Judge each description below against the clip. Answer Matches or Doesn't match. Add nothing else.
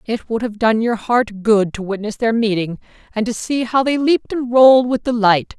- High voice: Matches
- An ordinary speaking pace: Doesn't match